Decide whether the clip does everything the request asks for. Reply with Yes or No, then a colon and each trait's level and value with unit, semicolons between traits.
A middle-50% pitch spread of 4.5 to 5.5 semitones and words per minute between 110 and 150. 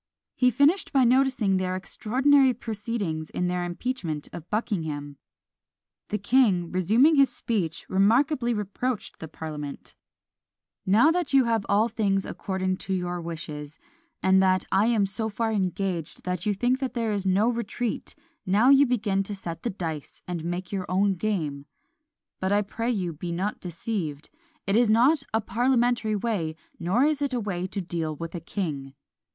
No: average, 5.0 semitones; average, 165 wpm